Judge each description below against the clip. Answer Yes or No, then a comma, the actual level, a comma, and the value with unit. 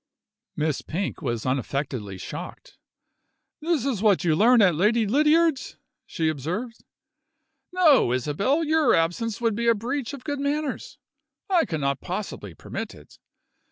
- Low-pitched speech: No, high, 215 Hz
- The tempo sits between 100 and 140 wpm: Yes, slow, 135 wpm